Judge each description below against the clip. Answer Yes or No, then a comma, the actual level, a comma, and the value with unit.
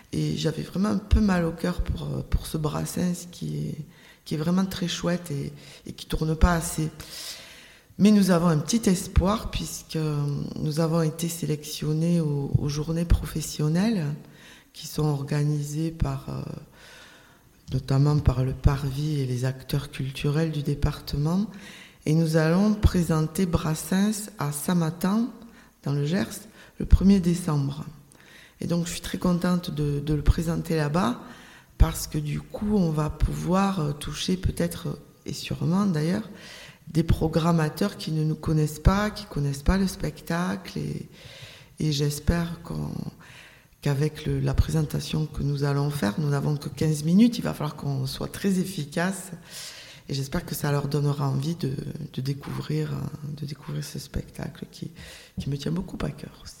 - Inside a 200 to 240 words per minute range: No, average, 155 wpm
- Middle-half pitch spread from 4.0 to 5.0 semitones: No, average, 3.3 semitones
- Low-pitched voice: No, medium, 155 Hz